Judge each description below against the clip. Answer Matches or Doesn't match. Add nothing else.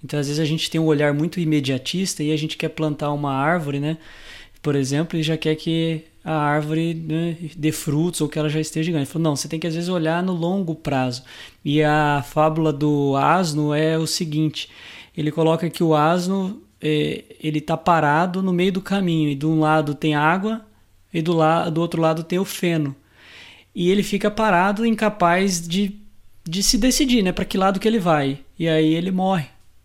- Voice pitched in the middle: Matches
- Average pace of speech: Doesn't match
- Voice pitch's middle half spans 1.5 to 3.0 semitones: Matches